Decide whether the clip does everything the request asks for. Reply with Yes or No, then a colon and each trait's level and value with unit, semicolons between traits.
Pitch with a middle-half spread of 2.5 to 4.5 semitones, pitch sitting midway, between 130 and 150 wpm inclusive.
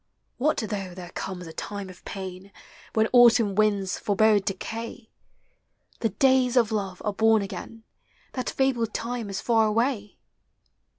No: average, 3.0 semitones; high, 215 Hz; average, 140 wpm